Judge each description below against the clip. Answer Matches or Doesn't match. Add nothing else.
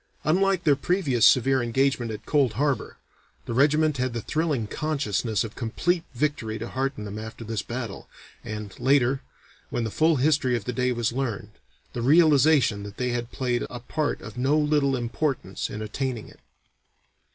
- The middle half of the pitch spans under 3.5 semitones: Doesn't match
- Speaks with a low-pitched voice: Matches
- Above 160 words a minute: Matches